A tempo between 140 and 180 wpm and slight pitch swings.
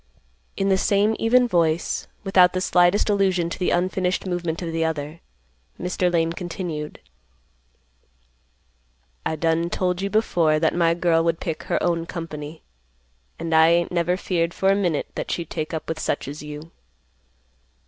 Yes: average, 160 wpm; narrow, 2.2 semitones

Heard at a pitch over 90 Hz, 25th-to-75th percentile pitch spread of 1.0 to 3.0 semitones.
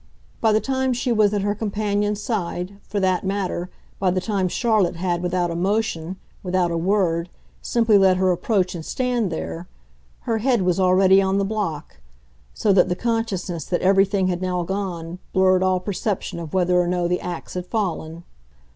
Yes: high, 190 Hz; narrow, 2.6 semitones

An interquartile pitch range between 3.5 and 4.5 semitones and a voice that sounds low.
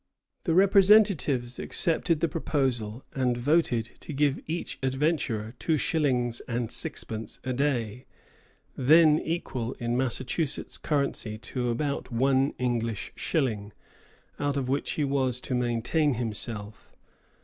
Yes: average, 4.1 semitones; low, 130 Hz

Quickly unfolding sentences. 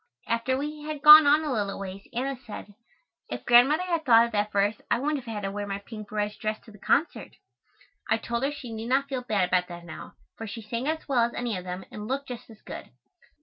Yes: fast, 245 wpm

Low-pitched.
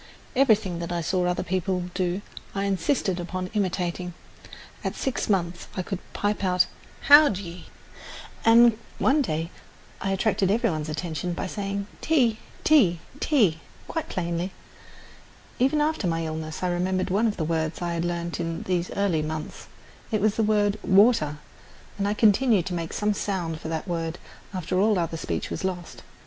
No: medium, 185 Hz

